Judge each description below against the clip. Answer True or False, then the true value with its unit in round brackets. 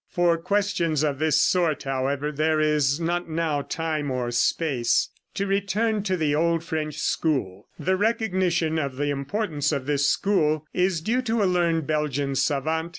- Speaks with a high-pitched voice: False (160 Hz)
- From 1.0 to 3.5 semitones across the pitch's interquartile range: False (3.9 semitones)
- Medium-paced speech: True (165 wpm)